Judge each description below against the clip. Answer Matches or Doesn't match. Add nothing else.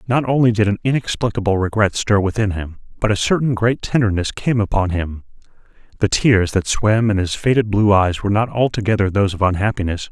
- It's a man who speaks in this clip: Matches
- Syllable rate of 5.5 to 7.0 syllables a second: Matches